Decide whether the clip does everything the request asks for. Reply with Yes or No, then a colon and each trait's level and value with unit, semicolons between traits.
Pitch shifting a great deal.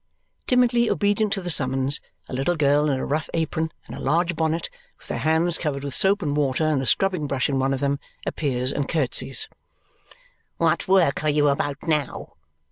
No: average, 3.6 semitones